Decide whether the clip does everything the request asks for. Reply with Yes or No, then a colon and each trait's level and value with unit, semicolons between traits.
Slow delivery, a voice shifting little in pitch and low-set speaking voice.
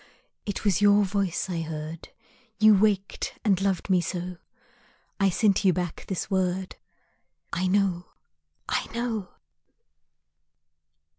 No: slow, 120 wpm; narrow, 2.1 semitones; high, 190 Hz